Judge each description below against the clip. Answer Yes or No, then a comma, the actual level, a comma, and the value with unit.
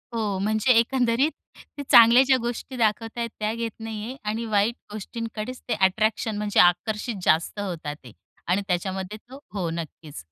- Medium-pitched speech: No, high, 215 Hz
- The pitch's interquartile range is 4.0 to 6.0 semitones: No, average, 3.5 semitones